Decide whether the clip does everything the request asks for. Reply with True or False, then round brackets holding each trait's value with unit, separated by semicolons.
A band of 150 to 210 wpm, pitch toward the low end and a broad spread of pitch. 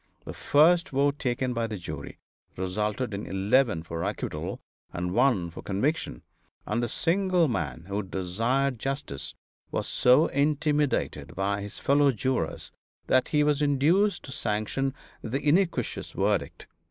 False (140 wpm; 125 Hz; 6.5 semitones)